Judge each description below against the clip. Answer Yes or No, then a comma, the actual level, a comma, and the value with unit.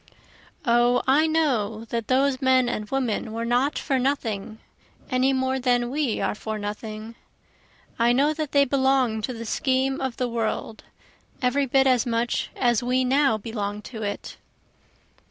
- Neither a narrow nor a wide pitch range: Yes, average, 3.0 semitones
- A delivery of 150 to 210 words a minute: Yes, average, 155 wpm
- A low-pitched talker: No, very high, 250 Hz